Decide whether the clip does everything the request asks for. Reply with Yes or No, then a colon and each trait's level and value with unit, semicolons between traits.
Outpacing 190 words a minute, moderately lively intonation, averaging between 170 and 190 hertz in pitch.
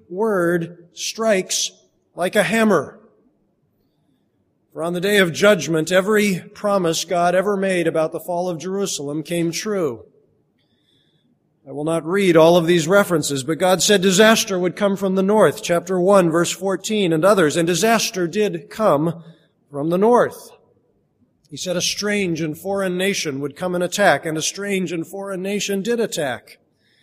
No: average, 160 wpm; average, 3.3 semitones; medium, 185 Hz